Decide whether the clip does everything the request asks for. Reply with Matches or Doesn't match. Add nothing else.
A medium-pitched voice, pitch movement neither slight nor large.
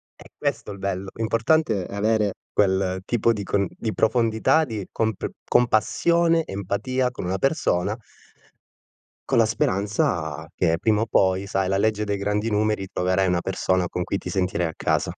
Doesn't match